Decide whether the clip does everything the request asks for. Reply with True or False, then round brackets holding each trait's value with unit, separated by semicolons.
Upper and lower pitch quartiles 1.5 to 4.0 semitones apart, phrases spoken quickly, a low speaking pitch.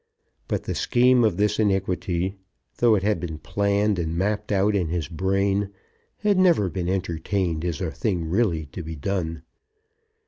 False (3.5 semitones; 165 wpm; 95 Hz)